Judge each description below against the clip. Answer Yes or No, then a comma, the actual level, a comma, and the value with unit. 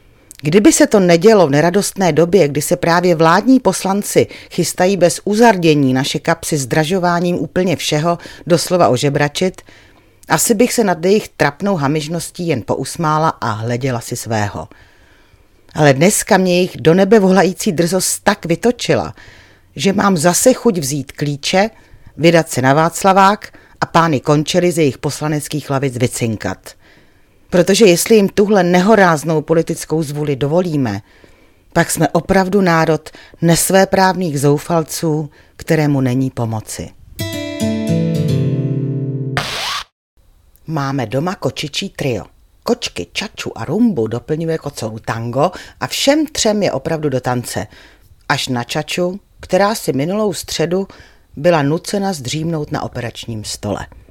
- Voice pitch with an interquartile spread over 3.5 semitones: Yes, wide, 5.5 semitones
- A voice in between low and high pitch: Yes, medium, 160 Hz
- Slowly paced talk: No, average, 125 wpm